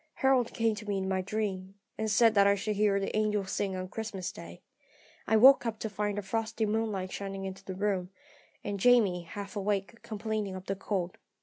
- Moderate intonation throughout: No, narrow, 2.2 semitones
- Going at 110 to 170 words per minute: No, fast, 205 wpm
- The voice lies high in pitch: Yes, high, 205 Hz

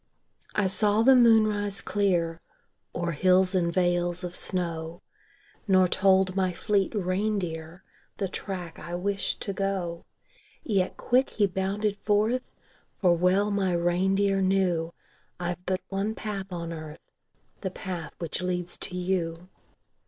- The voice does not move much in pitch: Yes, narrow, 2.3 semitones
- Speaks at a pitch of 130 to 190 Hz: Yes, medium, 185 Hz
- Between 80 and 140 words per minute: Yes, slow, 135 wpm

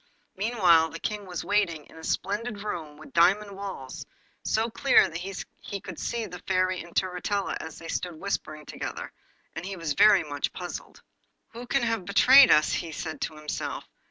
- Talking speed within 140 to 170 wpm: No, average, 180 wpm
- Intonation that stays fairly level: No, average, 4.1 semitones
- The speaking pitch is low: No, medium, 185 Hz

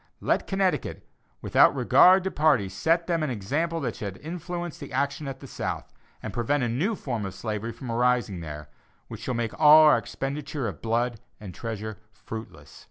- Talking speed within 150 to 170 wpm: No, average, 180 wpm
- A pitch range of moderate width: No, wide, 6.0 semitones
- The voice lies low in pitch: Yes, low, 125 Hz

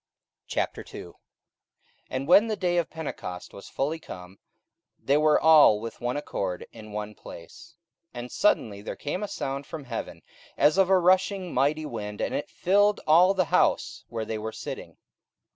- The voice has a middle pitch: Yes, medium, 145 Hz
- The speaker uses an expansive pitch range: Yes, wide, 8.2 semitones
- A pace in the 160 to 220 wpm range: Yes, average, 170 wpm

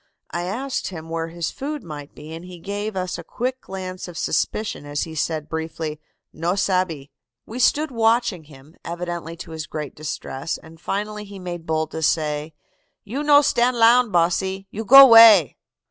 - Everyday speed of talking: Yes, average, 175 wpm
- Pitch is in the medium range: Yes, medium, 180 Hz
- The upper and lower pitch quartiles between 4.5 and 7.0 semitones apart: Yes, average, 5.3 semitones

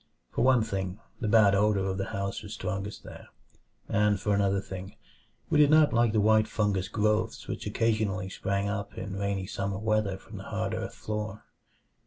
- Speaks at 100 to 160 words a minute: No, average, 185 wpm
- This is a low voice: Yes, low, 100 Hz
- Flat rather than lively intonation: Yes, narrow, 1.9 semitones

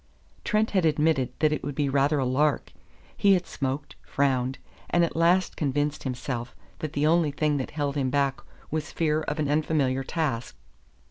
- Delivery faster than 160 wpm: Yes, average, 180 wpm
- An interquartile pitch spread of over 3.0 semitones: No, average, 2.7 semitones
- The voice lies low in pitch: No, medium, 145 Hz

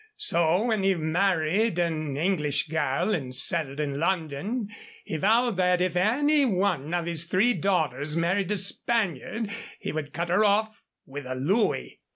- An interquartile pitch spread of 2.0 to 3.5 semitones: No, average, 4.7 semitones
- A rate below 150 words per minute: No, average, 160 wpm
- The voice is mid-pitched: Yes, medium, 175 Hz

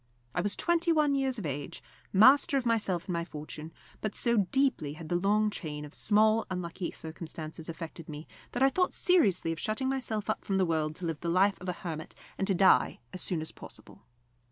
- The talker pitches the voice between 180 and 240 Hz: Yes, medium, 185 Hz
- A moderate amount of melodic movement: No, wide, 5.7 semitones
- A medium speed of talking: No, fast, 215 wpm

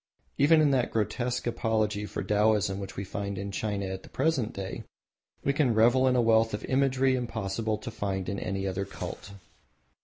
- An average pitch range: Yes, average, 4.2 semitones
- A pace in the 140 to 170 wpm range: No, average, 185 wpm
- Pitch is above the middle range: No, low, 110 Hz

